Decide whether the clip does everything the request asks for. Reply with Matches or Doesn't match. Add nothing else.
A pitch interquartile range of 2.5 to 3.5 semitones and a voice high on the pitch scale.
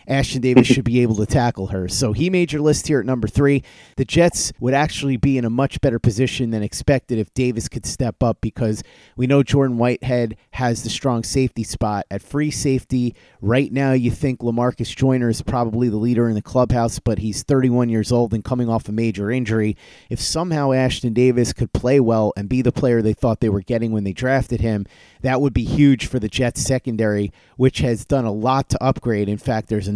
Doesn't match